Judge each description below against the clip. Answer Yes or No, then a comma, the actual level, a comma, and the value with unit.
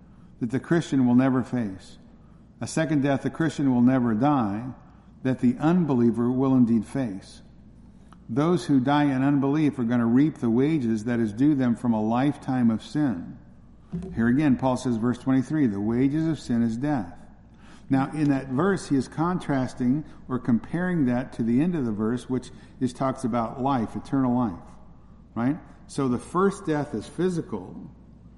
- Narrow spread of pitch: No, average, 3.6 semitones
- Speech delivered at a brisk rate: No, average, 175 wpm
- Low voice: Yes, low, 130 Hz